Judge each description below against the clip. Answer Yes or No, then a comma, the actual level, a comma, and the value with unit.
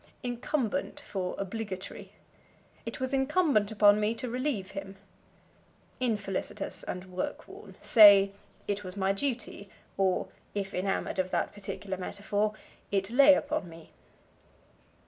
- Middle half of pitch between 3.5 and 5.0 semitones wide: Yes, average, 4.3 semitones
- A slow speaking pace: Yes, slow, 125 wpm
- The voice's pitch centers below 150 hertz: No, high, 205 Hz